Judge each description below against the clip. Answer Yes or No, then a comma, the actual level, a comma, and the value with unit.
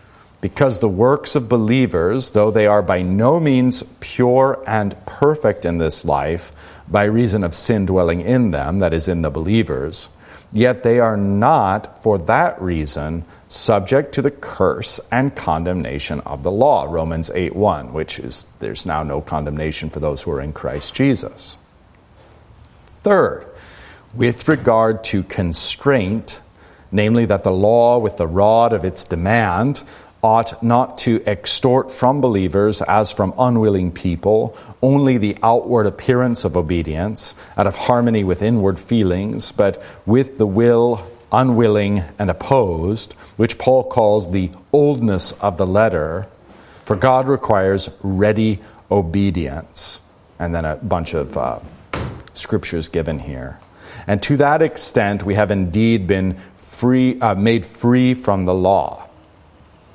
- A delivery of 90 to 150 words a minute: Yes, average, 140 wpm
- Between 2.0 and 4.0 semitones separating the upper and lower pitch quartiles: No, average, 4.7 semitones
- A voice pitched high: No, low, 105 Hz